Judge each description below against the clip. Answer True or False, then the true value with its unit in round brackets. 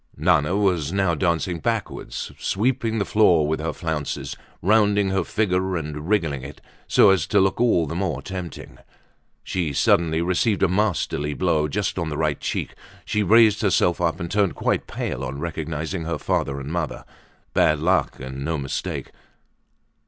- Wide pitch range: False (4.0 semitones)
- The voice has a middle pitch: False (85 Hz)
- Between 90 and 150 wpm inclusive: False (165 wpm)